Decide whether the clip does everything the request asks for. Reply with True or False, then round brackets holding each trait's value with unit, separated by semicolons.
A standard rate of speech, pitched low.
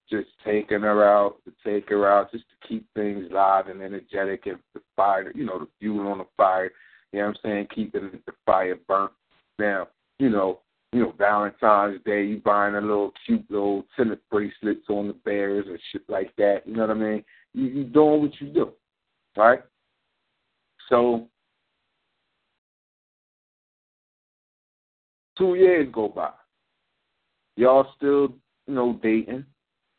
True (155 wpm; 105 Hz)